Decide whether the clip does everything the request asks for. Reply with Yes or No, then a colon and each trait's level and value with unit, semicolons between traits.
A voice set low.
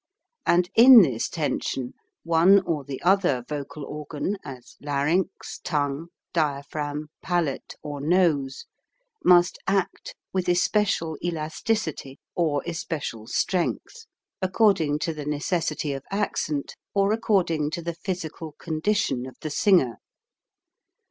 No: medium, 160 Hz